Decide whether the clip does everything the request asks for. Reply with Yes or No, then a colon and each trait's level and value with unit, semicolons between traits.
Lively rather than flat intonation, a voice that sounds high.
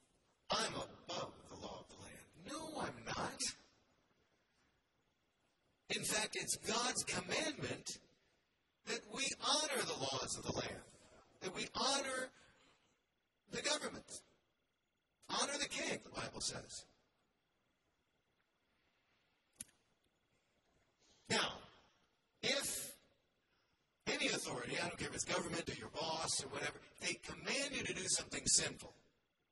Yes: wide, 5.9 semitones; high, 230 Hz